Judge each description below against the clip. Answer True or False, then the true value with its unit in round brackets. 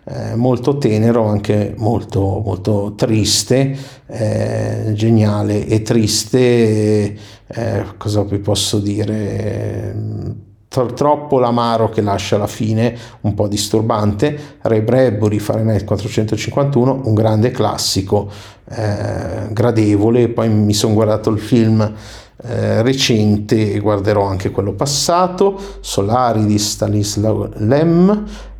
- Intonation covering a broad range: False (2.4 semitones)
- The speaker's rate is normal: False (110 wpm)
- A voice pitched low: True (110 Hz)